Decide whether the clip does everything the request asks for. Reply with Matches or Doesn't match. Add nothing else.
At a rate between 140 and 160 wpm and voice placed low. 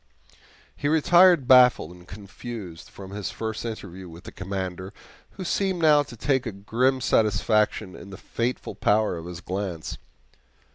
Matches